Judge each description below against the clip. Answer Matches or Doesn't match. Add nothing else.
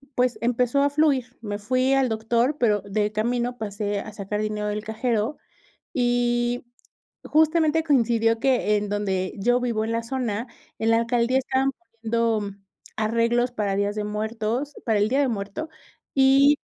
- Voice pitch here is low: Doesn't match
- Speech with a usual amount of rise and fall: Matches